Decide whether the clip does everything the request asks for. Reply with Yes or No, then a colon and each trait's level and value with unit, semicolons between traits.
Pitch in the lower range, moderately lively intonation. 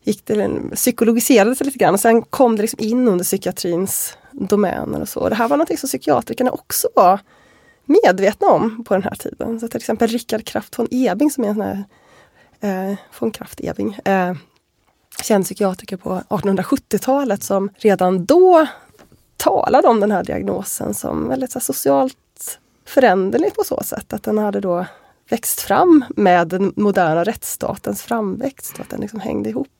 No: high, 215 Hz; average, 4.6 semitones